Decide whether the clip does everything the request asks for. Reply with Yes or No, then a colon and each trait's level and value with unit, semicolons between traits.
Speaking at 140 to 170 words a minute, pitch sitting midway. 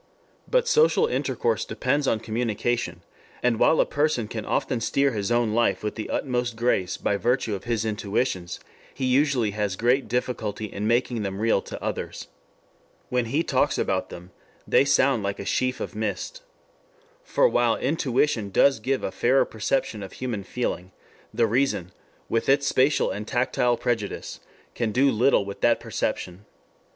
No: average, 160 wpm; low, 120 Hz